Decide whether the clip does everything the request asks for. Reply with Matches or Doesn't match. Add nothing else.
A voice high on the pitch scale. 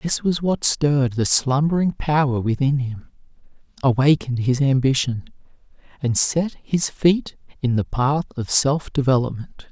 Doesn't match